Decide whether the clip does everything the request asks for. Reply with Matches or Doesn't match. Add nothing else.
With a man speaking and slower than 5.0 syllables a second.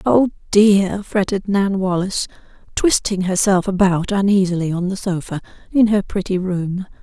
Doesn't match